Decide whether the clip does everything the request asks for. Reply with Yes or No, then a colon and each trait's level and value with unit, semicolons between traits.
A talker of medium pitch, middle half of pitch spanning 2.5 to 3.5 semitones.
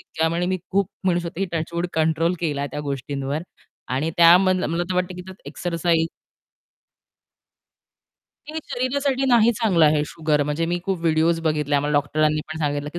Yes: medium, 165 Hz; average, 3.2 semitones